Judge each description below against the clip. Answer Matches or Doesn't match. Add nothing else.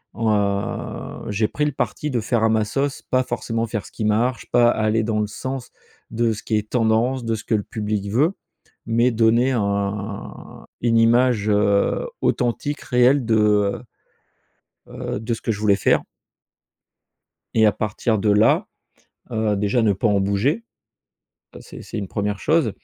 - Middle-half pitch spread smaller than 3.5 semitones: Matches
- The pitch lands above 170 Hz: Doesn't match